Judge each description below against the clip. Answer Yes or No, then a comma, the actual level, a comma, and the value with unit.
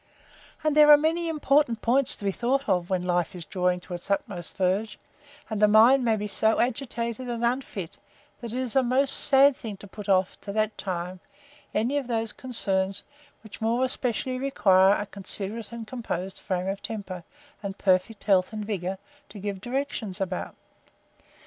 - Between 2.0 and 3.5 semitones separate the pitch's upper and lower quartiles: No, average, 4.7 semitones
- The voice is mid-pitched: No, high, 215 Hz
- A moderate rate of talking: Yes, average, 180 wpm